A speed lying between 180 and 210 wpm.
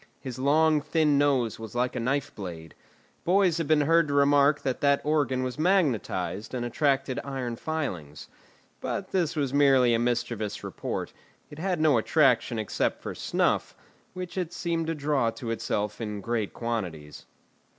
No: average, 160 wpm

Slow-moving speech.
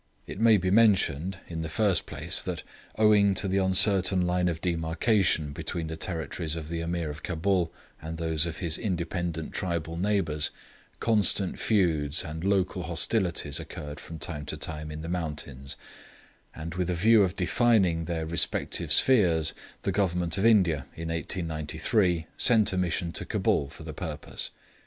No: average, 160 wpm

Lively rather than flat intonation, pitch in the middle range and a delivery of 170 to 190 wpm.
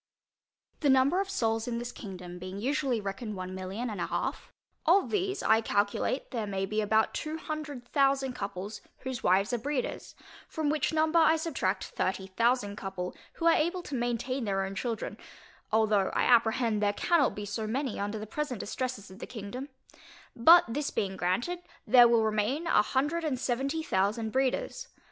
No: wide, 5.7 semitones; high, 235 Hz; average, 180 wpm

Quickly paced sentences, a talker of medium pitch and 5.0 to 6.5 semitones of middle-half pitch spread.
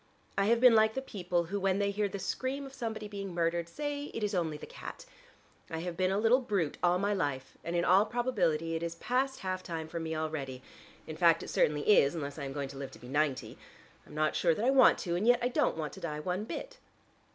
Yes: fast, 255 wpm; medium, 180 Hz; wide, 5.4 semitones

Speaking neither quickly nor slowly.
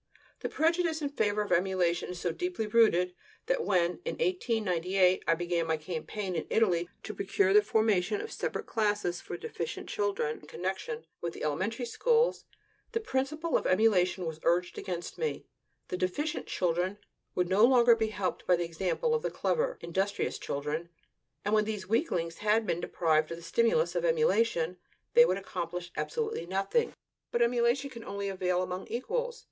Yes: average, 170 wpm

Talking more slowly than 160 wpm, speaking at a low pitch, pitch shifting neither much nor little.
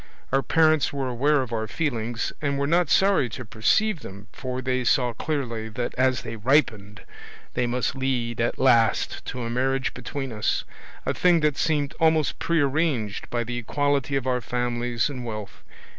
No: average, 175 wpm; low, 130 Hz; average, 3.3 semitones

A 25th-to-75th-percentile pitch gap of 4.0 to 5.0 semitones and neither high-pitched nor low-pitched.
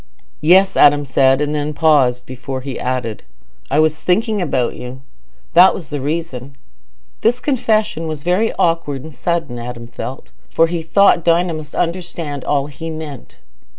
Yes: average, 4.3 semitones; medium, 150 Hz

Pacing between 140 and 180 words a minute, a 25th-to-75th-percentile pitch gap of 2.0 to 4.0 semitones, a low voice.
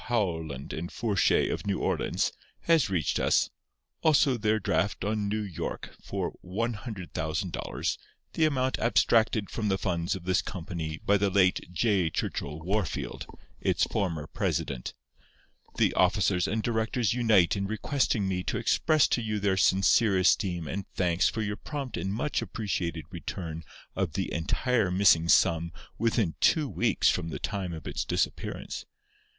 No: average, 150 wpm; average, 4.5 semitones; very low, 95 Hz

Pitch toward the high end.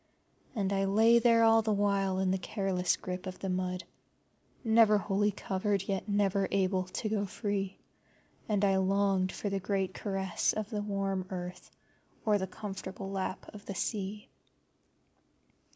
Yes: high, 195 Hz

